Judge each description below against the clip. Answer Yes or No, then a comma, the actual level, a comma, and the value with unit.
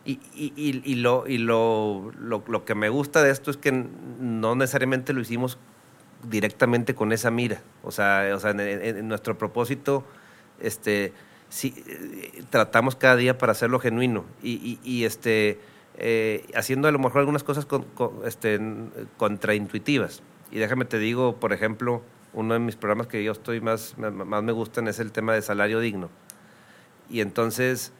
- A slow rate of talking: No, average, 175 wpm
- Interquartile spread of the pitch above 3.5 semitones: No, average, 2.8 semitones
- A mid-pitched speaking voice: No, low, 115 Hz